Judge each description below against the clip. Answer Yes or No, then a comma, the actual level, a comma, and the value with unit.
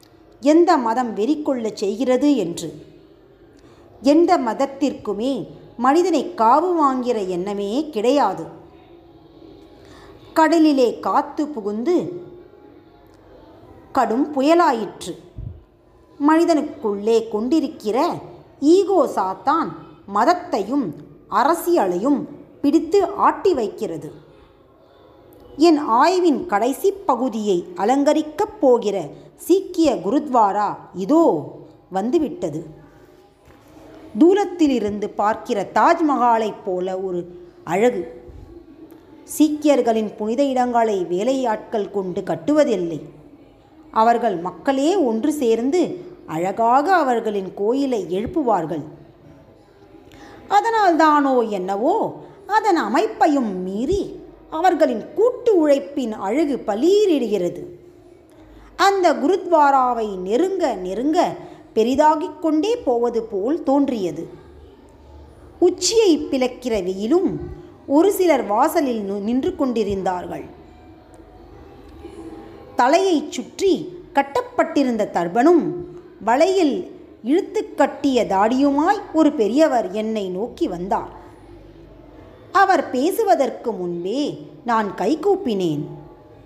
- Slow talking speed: Yes, slow, 70 wpm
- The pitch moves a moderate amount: No, wide, 7.6 semitones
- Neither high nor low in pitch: No, very high, 280 Hz